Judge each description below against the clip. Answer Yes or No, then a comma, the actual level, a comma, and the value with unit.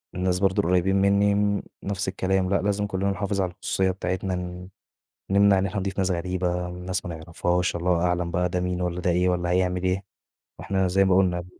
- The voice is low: Yes, very low, 90 Hz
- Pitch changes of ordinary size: No, narrow, 1.4 semitones